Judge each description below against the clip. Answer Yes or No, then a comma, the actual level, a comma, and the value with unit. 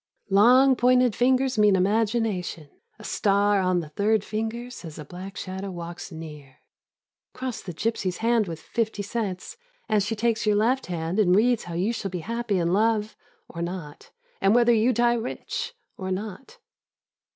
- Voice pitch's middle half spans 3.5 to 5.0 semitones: Yes, average, 4.2 semitones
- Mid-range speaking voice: No, high, 210 Hz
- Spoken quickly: No, average, 170 wpm